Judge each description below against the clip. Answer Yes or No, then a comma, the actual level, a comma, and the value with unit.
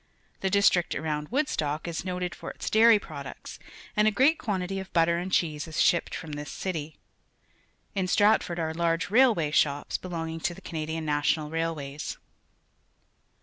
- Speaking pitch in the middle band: Yes, medium, 170 Hz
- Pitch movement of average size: Yes, average, 3.7 semitones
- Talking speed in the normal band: Yes, average, 160 wpm